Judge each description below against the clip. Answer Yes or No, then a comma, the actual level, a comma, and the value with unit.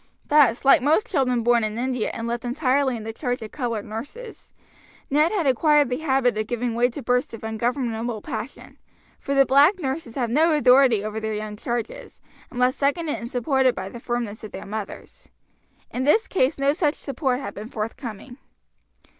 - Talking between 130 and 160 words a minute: No, average, 185 wpm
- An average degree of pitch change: Yes, average, 3.6 semitones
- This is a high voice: Yes, very high, 250 Hz